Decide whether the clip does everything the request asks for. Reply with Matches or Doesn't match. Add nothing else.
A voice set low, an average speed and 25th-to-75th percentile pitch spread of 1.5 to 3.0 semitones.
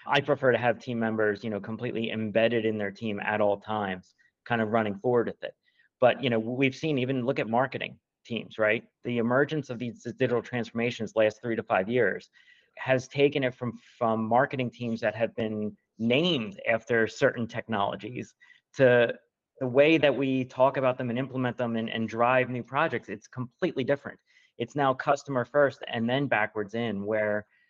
Matches